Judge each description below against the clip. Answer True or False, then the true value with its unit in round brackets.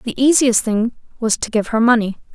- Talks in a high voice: True (230 Hz)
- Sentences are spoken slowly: False (205 wpm)